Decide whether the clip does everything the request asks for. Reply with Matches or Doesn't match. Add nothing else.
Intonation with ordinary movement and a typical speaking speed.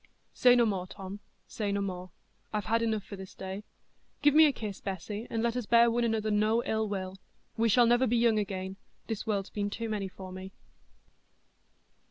Matches